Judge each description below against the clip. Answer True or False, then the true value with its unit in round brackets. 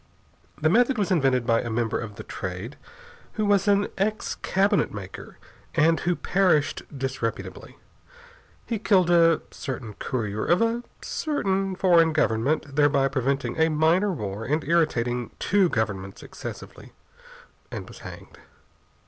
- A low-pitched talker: False (155 Hz)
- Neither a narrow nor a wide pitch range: False (8.0 semitones)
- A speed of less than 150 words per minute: True (135 wpm)